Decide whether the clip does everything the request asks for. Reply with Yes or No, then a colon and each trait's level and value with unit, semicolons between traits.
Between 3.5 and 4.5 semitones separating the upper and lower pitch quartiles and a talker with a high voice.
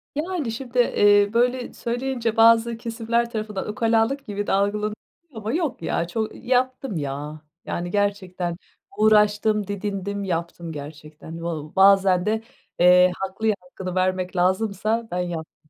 Yes: average, 4.1 semitones; high, 205 Hz